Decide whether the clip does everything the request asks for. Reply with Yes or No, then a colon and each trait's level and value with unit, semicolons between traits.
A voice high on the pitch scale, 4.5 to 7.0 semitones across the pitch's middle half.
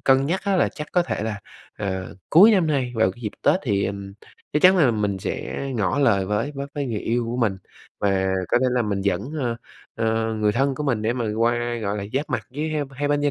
No: low, 120 Hz; wide, 5.5 semitones